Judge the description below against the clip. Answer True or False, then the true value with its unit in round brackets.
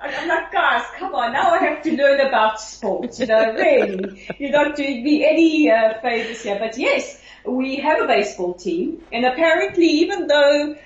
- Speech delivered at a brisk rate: False (190 wpm)